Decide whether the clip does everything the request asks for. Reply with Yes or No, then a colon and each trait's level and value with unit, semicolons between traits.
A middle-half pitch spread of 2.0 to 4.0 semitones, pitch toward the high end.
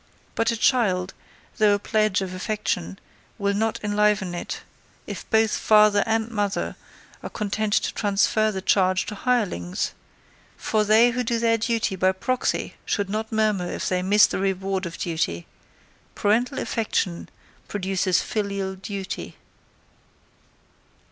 Yes: narrow, 2.5 semitones; high, 205 Hz